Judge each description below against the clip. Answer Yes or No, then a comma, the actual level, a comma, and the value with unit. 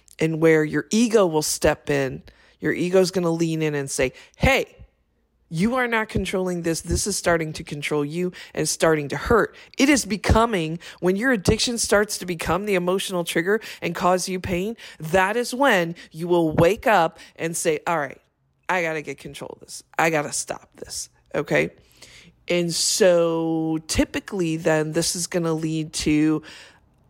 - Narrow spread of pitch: No, average, 3.1 semitones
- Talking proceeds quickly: No, average, 175 wpm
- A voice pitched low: No, medium, 170 Hz